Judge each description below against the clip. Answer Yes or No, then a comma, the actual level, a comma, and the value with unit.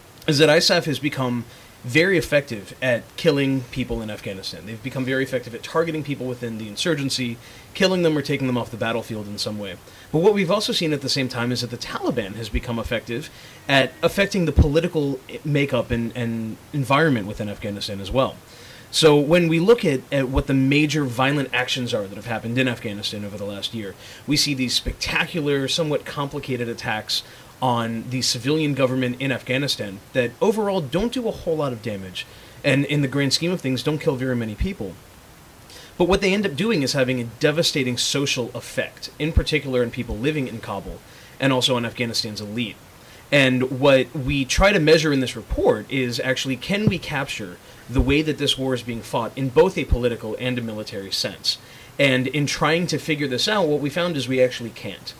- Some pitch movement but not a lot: Yes, average, 3.9 semitones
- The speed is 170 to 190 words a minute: No, average, 200 wpm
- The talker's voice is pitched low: Yes, low, 130 Hz